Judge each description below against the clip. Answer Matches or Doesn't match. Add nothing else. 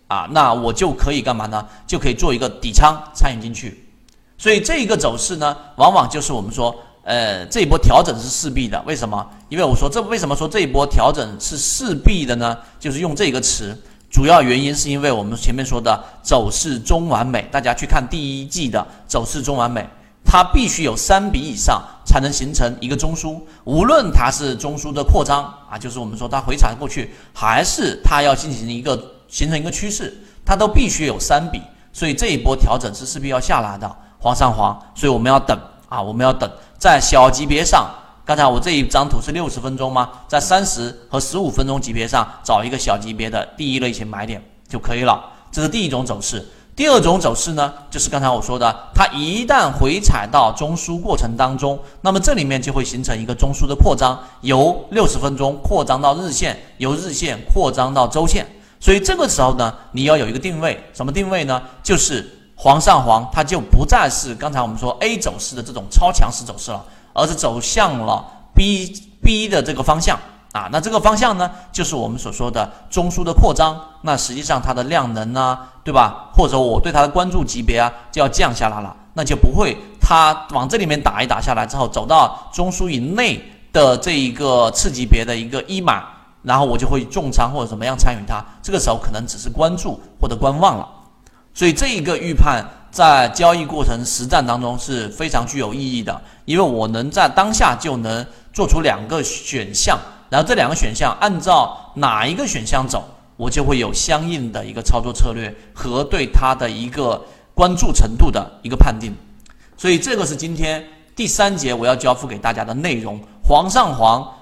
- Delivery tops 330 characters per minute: Doesn't match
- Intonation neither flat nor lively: Matches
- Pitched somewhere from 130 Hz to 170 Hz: Matches